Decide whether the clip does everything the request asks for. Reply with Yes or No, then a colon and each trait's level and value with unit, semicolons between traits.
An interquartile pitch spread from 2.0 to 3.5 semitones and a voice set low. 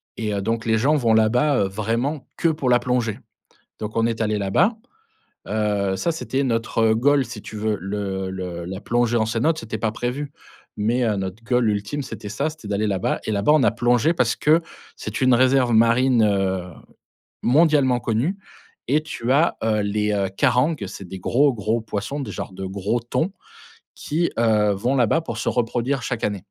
No: average, 3.9 semitones; low, 115 Hz